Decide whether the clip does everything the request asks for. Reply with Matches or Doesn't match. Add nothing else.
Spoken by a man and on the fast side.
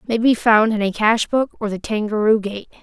Matches